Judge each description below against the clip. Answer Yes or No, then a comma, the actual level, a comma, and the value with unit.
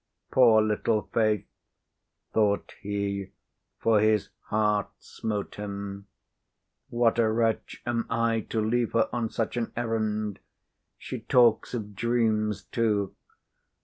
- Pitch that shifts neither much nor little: No, narrow, 1.8 semitones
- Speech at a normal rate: No, slow, 115 wpm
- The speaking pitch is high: No, low, 110 Hz